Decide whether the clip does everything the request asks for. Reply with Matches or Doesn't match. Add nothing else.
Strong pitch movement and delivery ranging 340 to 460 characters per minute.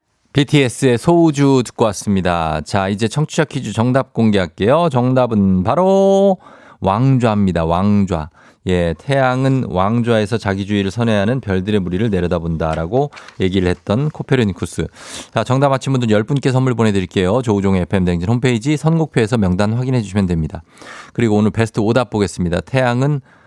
Matches